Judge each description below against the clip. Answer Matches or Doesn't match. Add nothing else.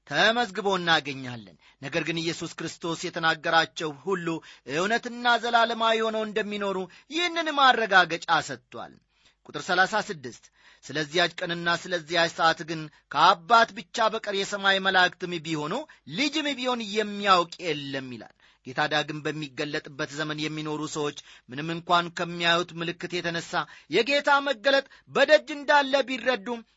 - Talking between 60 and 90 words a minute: Doesn't match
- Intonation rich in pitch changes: Matches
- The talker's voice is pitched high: Doesn't match